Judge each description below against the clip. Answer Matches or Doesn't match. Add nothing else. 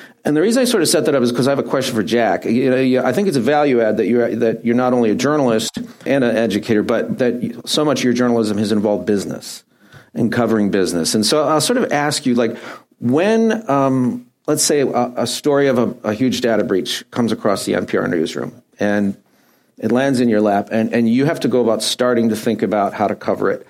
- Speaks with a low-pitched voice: Matches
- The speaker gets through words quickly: Matches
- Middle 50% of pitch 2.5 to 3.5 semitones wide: Matches